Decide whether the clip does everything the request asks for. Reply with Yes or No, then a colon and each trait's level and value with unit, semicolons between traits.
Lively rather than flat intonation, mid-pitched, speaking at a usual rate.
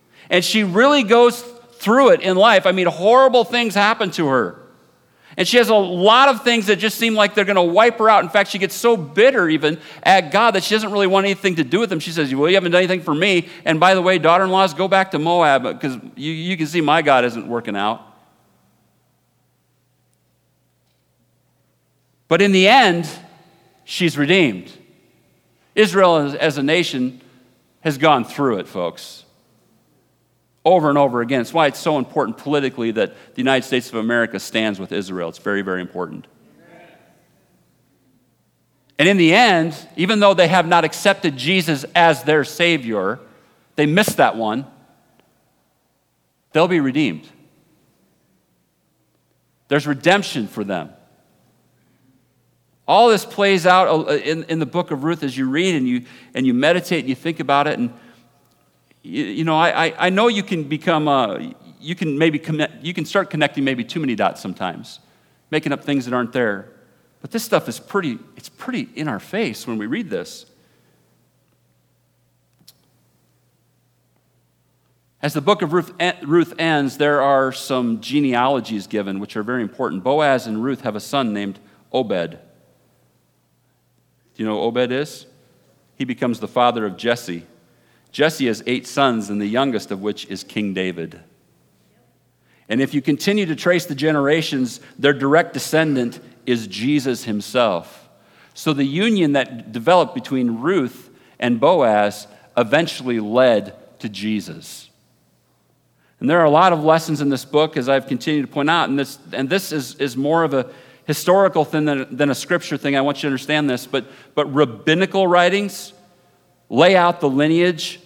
Yes: wide, 6.4 semitones; medium, 155 Hz; average, 170 wpm